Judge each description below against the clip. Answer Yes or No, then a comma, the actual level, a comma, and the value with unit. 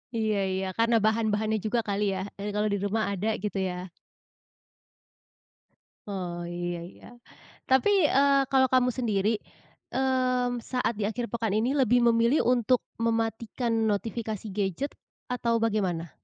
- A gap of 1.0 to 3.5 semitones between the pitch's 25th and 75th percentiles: Yes, average, 3.2 semitones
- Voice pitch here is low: No, high, 225 Hz